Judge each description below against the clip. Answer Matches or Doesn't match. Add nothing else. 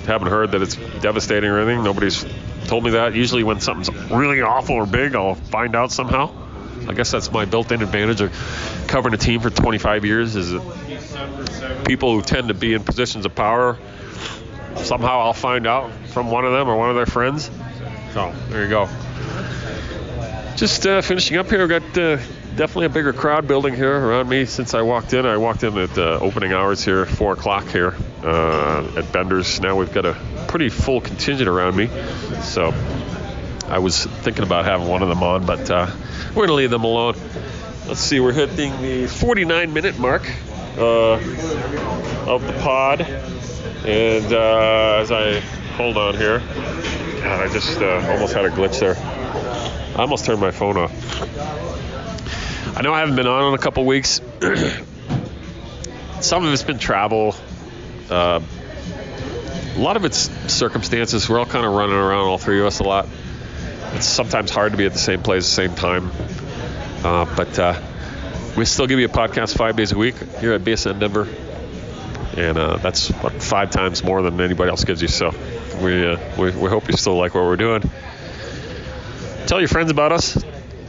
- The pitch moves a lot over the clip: Doesn't match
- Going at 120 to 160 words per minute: Doesn't match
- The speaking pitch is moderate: Doesn't match